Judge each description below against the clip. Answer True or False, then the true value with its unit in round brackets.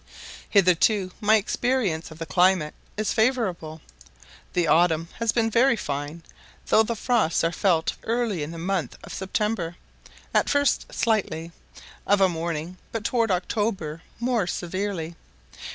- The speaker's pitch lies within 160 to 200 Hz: True (185 Hz)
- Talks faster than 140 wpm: False (135 wpm)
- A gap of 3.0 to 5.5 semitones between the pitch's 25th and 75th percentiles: True (5.1 semitones)